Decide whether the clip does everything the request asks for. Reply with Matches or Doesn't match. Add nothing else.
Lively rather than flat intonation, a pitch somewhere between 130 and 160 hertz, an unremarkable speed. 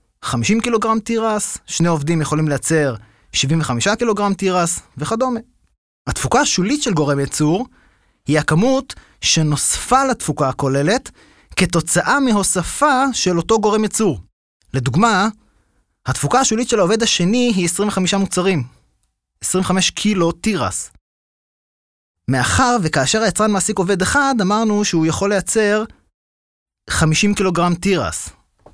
Doesn't match